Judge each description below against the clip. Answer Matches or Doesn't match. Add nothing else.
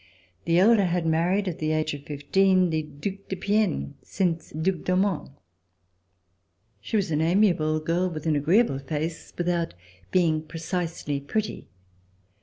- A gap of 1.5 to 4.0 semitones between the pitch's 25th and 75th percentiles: Matches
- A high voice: Doesn't match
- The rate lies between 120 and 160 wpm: Matches